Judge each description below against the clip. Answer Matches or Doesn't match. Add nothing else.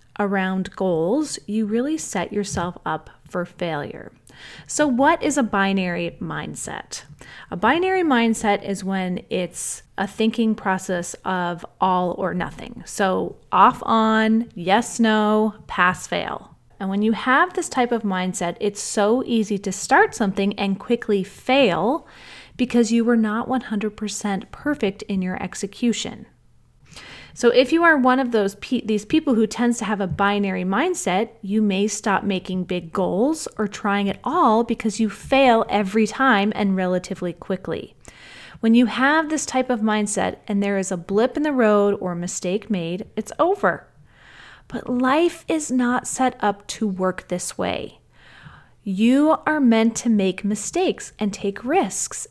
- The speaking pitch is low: Doesn't match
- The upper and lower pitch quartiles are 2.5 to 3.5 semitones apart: Doesn't match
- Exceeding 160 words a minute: Doesn't match